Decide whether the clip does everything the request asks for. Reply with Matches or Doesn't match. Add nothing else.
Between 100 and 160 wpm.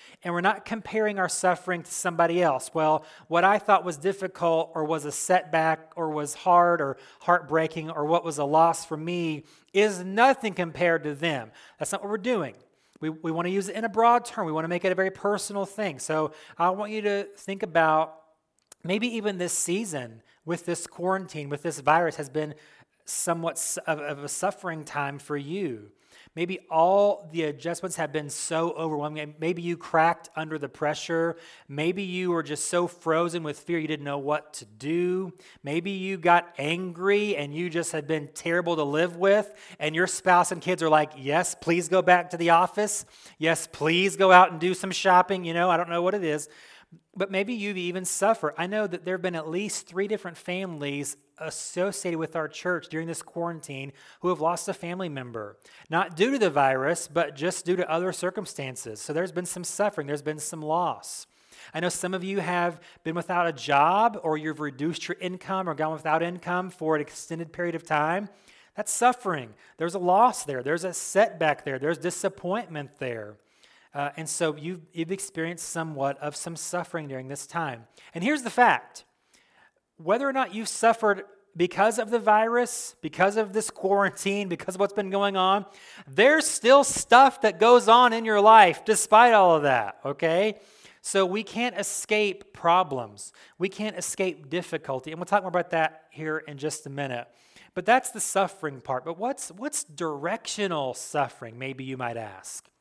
Doesn't match